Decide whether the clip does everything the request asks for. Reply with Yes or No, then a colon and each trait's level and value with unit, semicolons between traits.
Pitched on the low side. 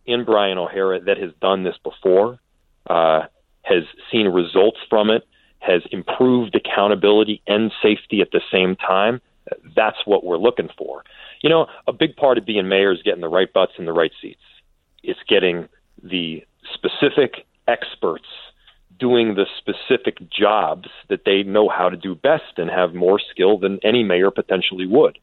Yes: very low, 95 Hz